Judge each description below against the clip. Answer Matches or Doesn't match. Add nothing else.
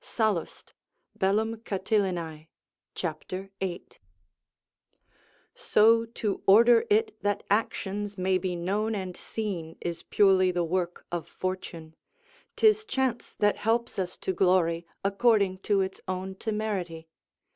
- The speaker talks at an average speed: Doesn't match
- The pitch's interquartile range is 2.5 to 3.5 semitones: Matches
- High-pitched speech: Matches